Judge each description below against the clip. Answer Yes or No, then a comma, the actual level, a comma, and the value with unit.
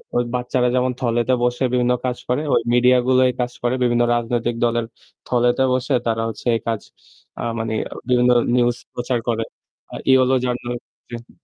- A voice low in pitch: Yes, low, 120 Hz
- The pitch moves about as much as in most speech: No, narrow, 0.9 semitones